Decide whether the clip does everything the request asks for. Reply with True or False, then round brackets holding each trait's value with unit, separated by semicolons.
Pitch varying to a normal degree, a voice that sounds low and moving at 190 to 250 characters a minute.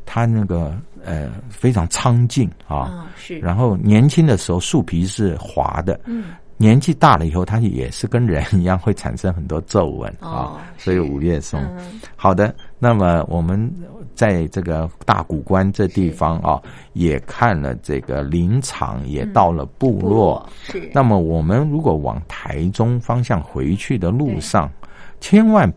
False (6.2 semitones; 95 Hz; 225 characters per minute)